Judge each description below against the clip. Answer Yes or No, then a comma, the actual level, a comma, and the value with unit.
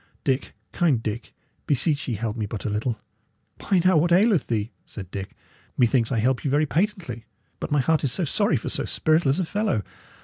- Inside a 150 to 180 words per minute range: No, average, 195 wpm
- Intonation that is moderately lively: No, wide, 6.6 semitones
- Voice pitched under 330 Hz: Yes, low, 135 Hz